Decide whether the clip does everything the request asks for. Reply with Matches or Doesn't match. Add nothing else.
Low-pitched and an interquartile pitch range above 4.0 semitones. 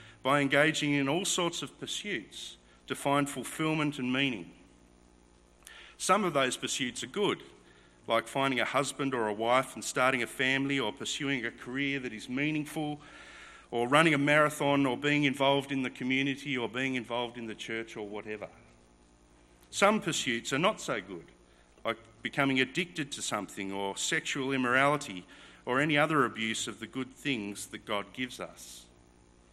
Matches